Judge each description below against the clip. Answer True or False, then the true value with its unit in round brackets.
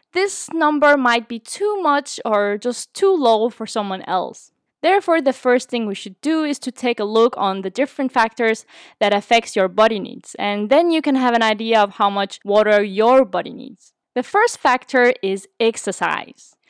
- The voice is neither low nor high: False (235 Hz)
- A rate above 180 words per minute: True (190 wpm)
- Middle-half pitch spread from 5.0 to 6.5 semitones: True (5.3 semitones)